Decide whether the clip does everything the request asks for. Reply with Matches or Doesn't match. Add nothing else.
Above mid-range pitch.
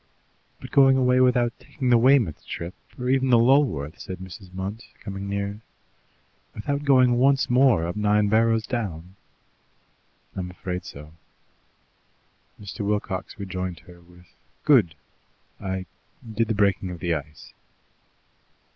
Doesn't match